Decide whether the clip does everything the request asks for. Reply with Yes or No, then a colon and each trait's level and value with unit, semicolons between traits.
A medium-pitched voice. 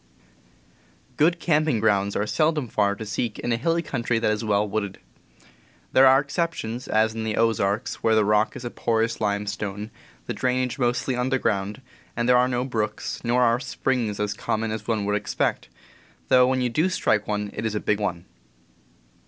No: low, 115 Hz